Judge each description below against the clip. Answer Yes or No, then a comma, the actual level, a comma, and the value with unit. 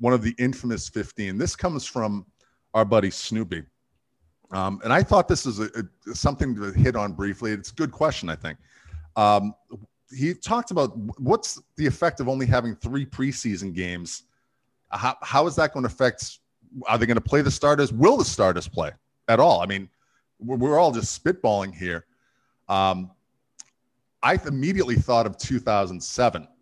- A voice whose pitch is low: Yes, low, 115 Hz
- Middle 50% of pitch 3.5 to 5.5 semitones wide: Yes, average, 4.7 semitones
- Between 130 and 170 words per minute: No, average, 180 wpm